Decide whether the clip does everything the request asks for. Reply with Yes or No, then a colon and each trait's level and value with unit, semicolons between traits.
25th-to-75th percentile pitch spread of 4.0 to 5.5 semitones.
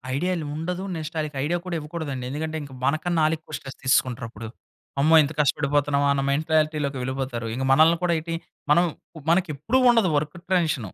No: average, 3.0 semitones